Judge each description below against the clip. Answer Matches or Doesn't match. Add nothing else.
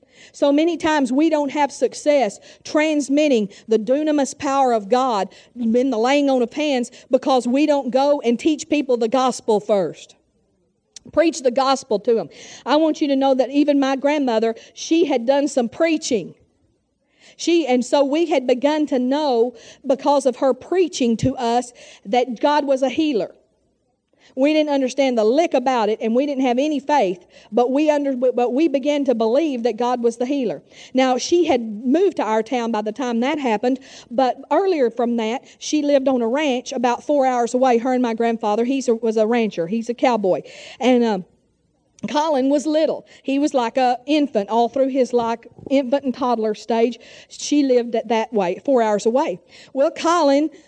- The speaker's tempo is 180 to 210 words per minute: Matches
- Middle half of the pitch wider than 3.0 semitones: Matches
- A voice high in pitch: Matches